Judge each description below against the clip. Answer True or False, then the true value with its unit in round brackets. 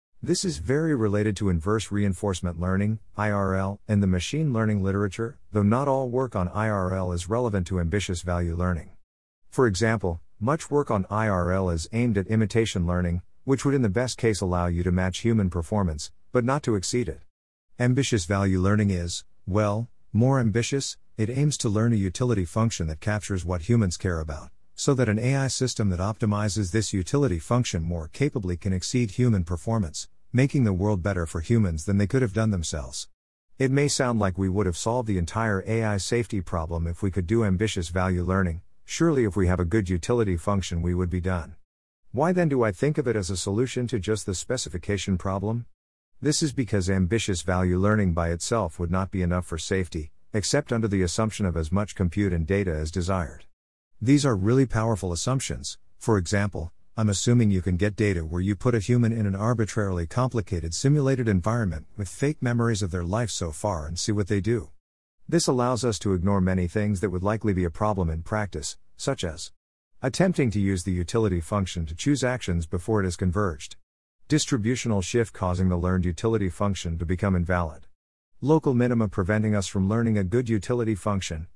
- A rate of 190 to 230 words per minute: True (195 wpm)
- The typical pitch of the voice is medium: False (100 Hz)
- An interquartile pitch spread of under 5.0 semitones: True (4.2 semitones)